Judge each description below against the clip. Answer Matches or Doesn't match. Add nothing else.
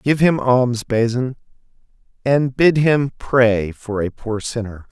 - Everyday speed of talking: Matches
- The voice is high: Doesn't match